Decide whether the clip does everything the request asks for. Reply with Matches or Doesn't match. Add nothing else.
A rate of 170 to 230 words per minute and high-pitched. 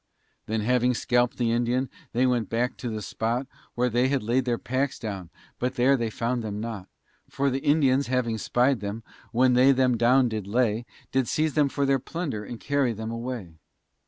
Doesn't match